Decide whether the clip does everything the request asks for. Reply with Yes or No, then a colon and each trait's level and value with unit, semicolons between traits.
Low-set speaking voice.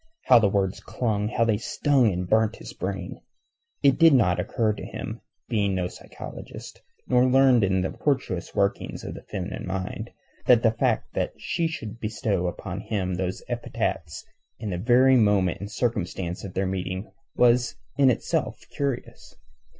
Yes: low, 105 Hz